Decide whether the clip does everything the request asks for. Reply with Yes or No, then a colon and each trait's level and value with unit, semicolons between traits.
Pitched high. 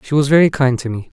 No: low, 135 Hz